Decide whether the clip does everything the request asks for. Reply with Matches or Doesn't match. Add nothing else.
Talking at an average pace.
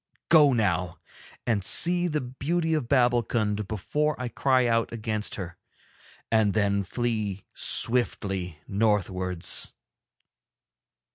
Doesn't match